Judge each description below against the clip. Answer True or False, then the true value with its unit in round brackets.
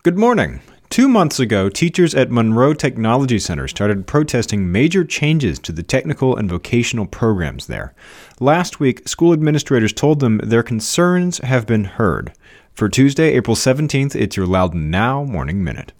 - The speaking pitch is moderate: False (130 Hz)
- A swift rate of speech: False (160 wpm)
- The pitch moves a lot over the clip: True (5.9 semitones)